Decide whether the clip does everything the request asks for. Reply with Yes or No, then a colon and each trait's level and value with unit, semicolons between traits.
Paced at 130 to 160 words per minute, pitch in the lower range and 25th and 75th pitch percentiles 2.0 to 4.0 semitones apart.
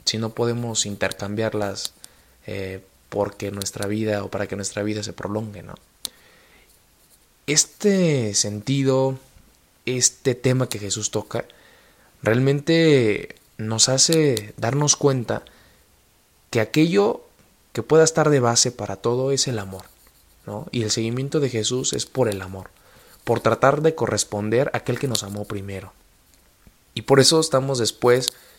No: average, 135 wpm; low, 115 Hz; average, 4.4 semitones